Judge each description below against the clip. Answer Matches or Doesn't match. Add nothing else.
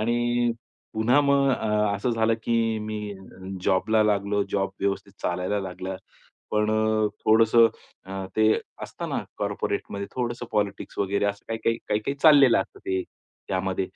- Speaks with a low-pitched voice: Matches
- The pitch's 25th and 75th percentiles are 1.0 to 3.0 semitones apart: Matches